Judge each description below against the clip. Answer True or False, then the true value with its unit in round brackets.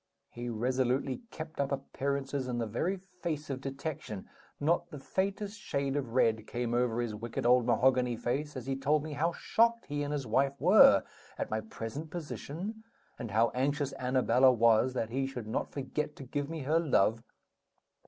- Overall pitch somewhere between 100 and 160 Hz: True (135 Hz)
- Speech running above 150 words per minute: True (180 wpm)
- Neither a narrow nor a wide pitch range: True (3.8 semitones)